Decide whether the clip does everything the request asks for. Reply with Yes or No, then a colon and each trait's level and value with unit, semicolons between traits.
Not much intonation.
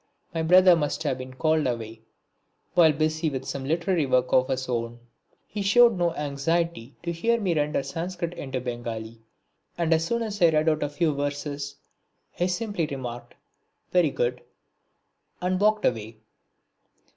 No: average, 5.0 semitones